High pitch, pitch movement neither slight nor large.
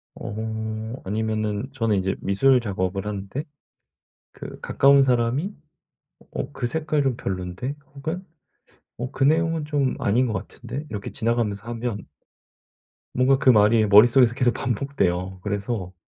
No: low, 115 Hz; average, 4.7 semitones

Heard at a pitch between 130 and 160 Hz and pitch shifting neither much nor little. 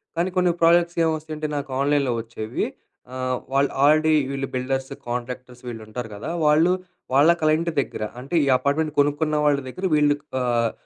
Yes: medium, 140 Hz; average, 3.5 semitones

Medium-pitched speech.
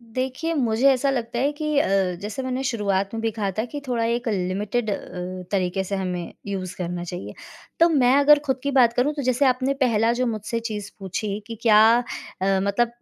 No: high, 230 Hz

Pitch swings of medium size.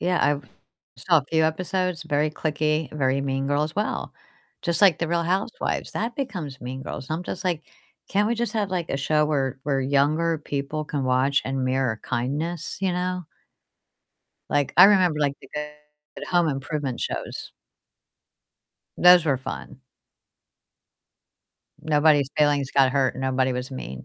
Yes: average, 4.0 semitones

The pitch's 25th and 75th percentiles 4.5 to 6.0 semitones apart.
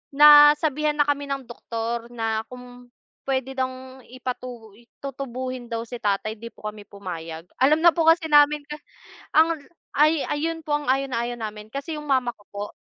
No: average, 4.1 semitones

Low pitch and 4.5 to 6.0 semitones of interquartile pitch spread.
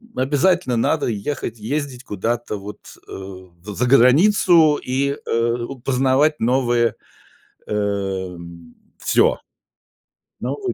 Yes: low, 120 Hz; average, 5.2 semitones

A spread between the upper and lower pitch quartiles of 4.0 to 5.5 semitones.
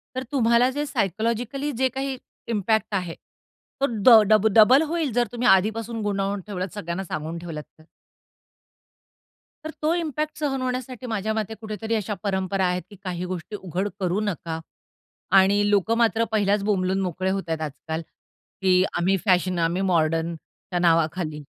Yes: average, 4.3 semitones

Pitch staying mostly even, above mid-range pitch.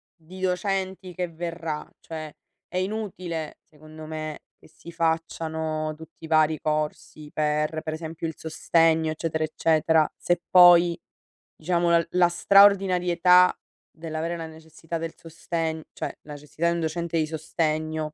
No: narrow, 1.7 semitones; medium, 160 Hz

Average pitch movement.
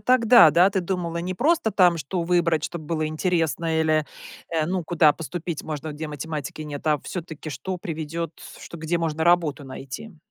No: narrow, 2.3 semitones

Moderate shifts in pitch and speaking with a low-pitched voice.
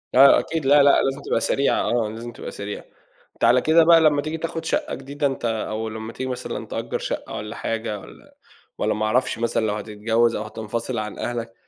Yes: average, 4.1 semitones; low, 115 Hz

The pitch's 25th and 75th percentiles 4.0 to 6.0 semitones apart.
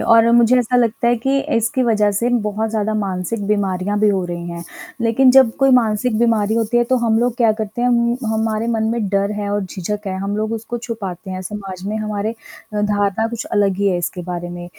No: narrow, 2.6 semitones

